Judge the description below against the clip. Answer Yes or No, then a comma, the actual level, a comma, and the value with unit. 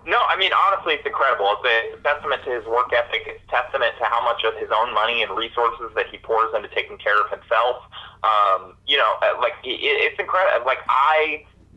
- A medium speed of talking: No, fast, 210 wpm